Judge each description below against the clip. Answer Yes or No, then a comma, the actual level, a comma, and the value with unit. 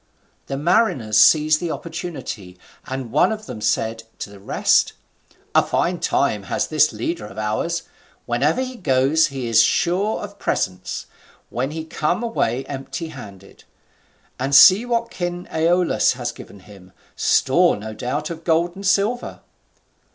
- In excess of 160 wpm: No, average, 150 wpm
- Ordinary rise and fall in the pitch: No, wide, 7.5 semitones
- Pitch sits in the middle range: Yes, medium, 150 Hz